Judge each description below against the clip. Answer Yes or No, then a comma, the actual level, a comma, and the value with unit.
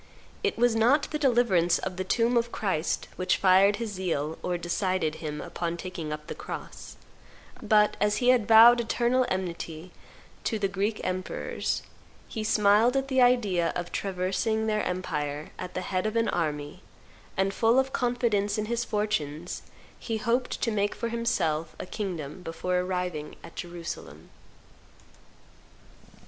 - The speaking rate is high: No, average, 155 wpm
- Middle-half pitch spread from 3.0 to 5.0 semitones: Yes, average, 4.7 semitones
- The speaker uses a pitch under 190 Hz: No, high, 195 Hz